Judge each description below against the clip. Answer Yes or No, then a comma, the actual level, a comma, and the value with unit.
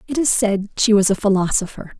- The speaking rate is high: Yes, fast, 210 wpm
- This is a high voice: Yes, high, 205 Hz